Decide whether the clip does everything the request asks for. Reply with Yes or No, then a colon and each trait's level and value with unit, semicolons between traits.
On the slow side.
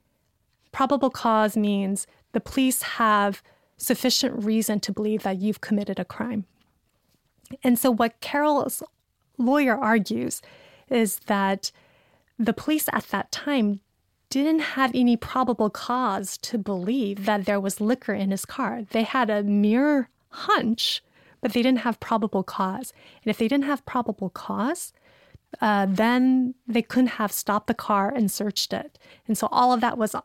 No: average, 155 wpm